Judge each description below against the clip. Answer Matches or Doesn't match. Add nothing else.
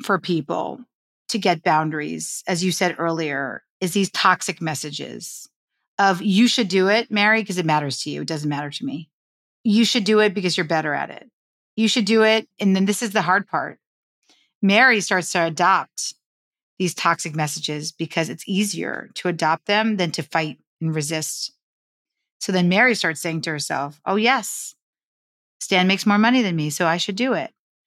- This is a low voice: Doesn't match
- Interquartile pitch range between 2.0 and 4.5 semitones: Doesn't match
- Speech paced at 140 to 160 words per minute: Doesn't match